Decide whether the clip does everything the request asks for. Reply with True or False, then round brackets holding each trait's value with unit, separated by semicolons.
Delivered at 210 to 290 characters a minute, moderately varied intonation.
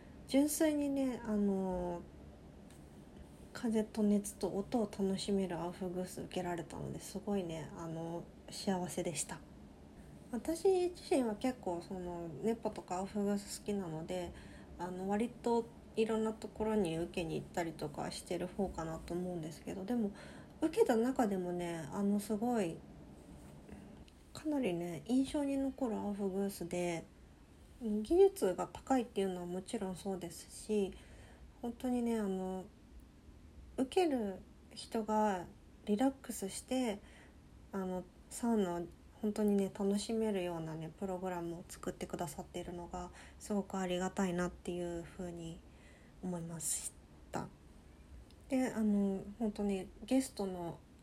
True (275 characters per minute; 4.0 semitones)